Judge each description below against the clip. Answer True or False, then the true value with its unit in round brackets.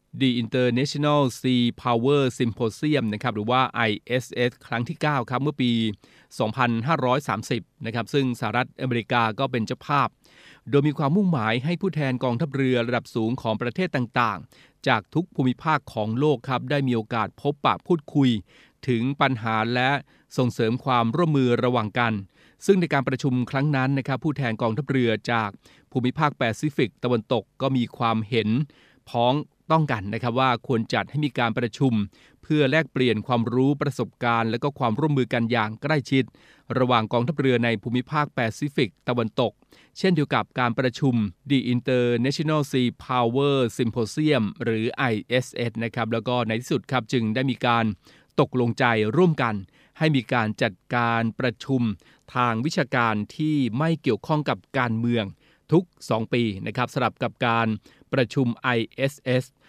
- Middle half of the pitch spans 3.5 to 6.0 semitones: False (3.0 semitones)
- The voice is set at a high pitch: False (125 Hz)